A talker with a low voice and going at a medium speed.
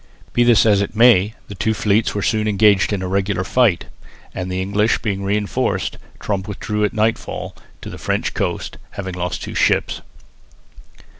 Yes: low, 105 Hz; average, 170 wpm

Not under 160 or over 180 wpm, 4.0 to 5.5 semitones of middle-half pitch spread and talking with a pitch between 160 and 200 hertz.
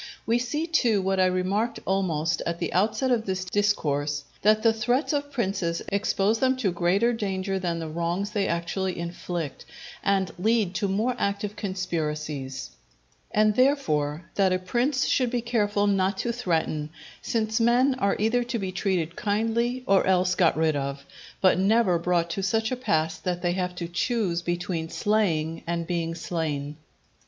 Yes: average, 165 wpm; average, 4.5 semitones; high, 190 Hz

